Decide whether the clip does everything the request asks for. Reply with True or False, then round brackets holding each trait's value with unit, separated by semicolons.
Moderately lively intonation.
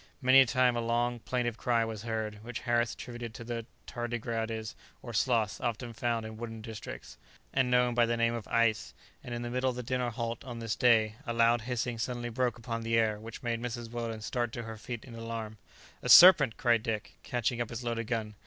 False (1.3 semitones)